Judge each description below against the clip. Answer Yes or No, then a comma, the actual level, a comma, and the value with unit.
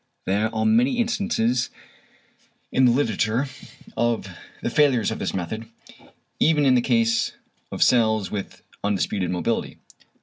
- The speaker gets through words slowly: Yes, slow, 130 wpm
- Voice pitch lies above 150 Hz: No, low, 115 Hz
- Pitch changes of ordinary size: Yes, average, 3.8 semitones